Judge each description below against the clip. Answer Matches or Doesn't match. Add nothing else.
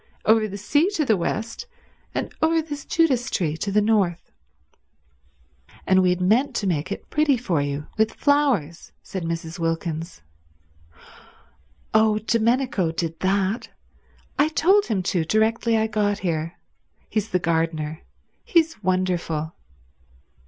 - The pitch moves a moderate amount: Doesn't match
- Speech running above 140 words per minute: Doesn't match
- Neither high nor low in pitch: Doesn't match